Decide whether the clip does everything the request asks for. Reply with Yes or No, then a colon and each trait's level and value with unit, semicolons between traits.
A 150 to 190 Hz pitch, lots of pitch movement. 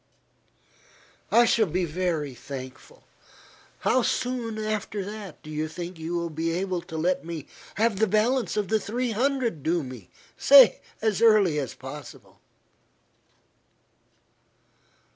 Yes: medium, 185 Hz; wide, 5.8 semitones